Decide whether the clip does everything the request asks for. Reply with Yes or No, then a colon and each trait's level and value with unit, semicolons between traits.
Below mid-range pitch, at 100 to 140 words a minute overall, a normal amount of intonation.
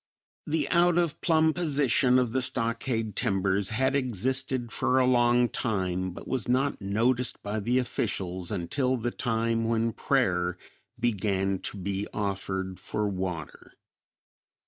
Yes: low, 115 Hz; slow, 135 wpm; average, 4.8 semitones